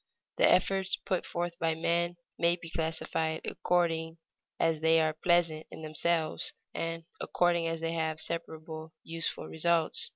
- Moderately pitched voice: Yes, medium, 165 Hz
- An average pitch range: No, narrow, 1.2 semitones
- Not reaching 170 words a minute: Yes, average, 140 wpm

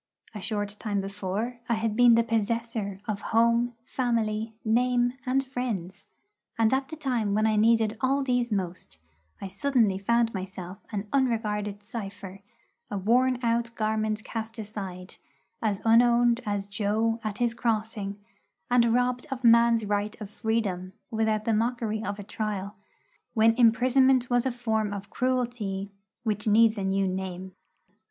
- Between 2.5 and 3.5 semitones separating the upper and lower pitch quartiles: Yes, average, 2.8 semitones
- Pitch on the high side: Yes, high, 220 Hz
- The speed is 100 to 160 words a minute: Yes, average, 150 wpm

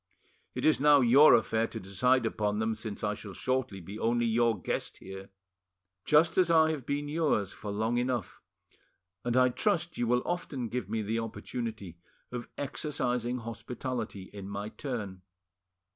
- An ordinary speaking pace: Yes, average, 160 wpm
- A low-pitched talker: Yes, low, 120 Hz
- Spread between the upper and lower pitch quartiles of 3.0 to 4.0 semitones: Yes, average, 3.7 semitones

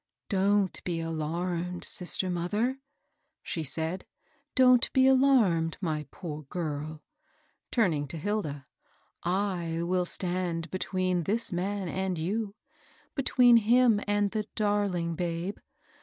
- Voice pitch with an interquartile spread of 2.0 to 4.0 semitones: Yes, average, 3.7 semitones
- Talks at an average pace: No, slow, 125 wpm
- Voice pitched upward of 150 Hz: Yes, medium, 185 Hz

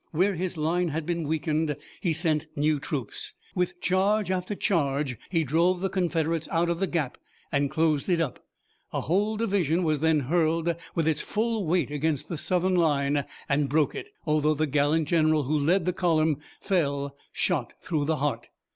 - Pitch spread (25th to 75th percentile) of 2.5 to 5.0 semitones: Yes, average, 3.1 semitones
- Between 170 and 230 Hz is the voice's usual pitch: No, medium, 160 Hz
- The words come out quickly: No, average, 180 wpm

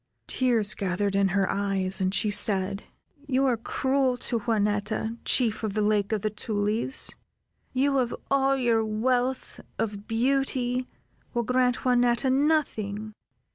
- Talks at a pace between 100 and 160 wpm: Yes, slow, 135 wpm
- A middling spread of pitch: Yes, average, 3.8 semitones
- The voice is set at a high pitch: Yes, high, 225 Hz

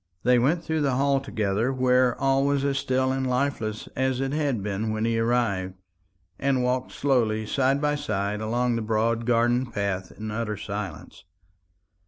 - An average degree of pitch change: Yes, average, 3.7 semitones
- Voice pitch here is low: Yes, low, 125 Hz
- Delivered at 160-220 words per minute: Yes, average, 170 wpm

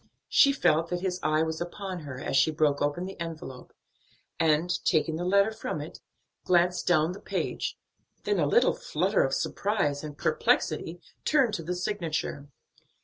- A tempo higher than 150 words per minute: Yes, average, 170 wpm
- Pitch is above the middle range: No, medium, 170 Hz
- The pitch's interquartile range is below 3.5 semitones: No, average, 3.8 semitones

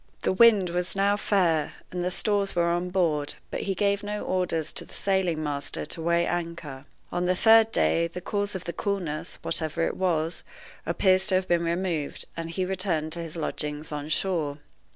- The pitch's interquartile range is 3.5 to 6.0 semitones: No, average, 2.9 semitones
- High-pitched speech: No, medium, 175 Hz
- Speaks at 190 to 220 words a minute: Yes, average, 195 wpm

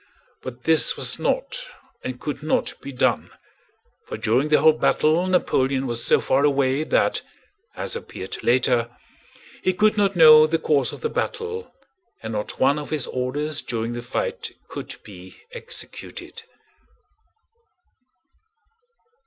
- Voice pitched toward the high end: No, medium, 145 Hz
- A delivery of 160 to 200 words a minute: No, slow, 135 wpm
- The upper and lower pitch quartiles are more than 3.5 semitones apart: Yes, wide, 5.5 semitones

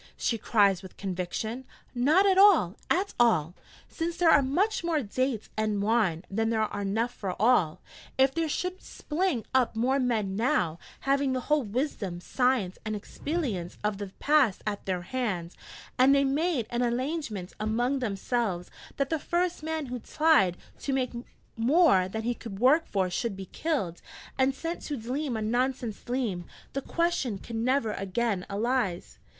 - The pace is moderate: Yes, average, 165 wpm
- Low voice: No, high, 240 Hz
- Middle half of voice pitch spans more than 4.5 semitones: Yes, wide, 5.6 semitones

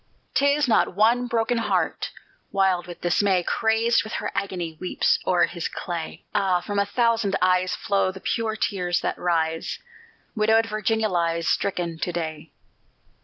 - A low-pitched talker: No, high, 195 Hz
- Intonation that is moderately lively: Yes, average, 4.1 semitones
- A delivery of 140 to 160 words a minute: Yes, average, 150 wpm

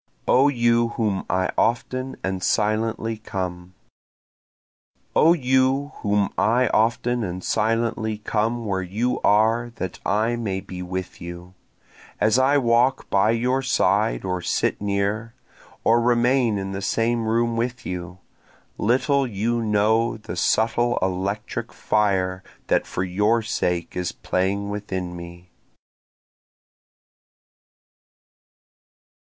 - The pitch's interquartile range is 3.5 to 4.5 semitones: Yes, average, 3.9 semitones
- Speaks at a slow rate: Yes, slow, 115 wpm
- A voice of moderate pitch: No, low, 110 Hz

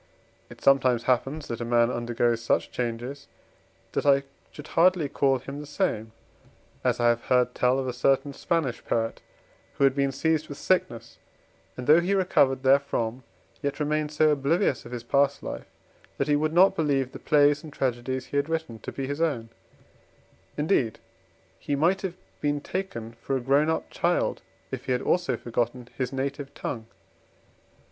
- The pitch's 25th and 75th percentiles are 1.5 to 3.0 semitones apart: No, average, 3.5 semitones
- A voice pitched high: No, medium, 140 Hz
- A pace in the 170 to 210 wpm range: Yes, average, 175 wpm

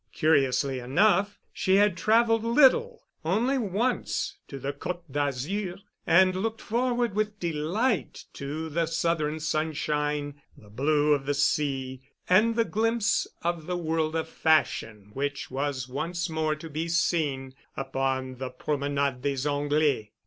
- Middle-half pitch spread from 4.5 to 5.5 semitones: Yes, average, 5.2 semitones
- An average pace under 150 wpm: Yes, slow, 135 wpm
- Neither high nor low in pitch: Yes, medium, 155 Hz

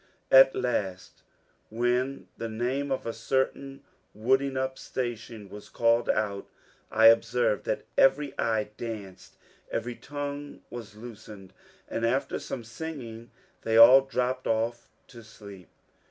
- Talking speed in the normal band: No, slow, 125 wpm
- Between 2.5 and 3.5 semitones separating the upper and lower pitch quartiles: Yes, average, 3.1 semitones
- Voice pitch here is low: Yes, low, 115 Hz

